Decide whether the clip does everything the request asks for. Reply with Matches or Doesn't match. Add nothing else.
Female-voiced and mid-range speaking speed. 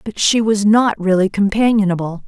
Matches